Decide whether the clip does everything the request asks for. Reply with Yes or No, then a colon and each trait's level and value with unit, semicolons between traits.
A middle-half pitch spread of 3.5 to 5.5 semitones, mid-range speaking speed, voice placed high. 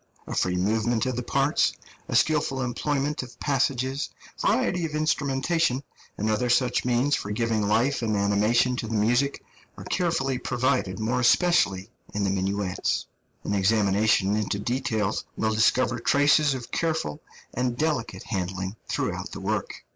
No: average, 4.5 semitones; average, 145 wpm; low, 120 Hz